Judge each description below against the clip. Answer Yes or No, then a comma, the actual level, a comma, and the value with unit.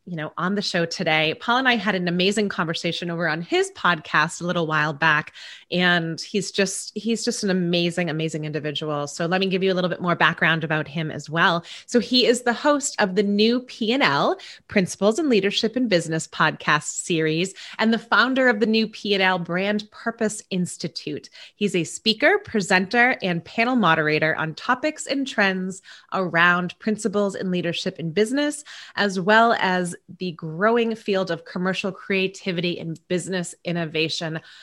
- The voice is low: No, medium, 185 Hz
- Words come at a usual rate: Yes, average, 180 wpm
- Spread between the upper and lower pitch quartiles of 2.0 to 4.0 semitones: No, average, 4.5 semitones